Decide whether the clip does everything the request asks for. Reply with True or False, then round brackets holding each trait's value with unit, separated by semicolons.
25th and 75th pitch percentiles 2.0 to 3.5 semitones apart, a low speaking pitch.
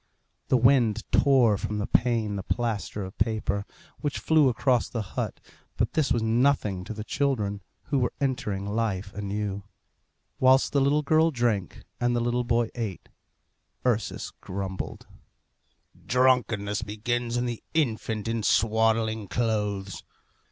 True (3.2 semitones; 115 Hz)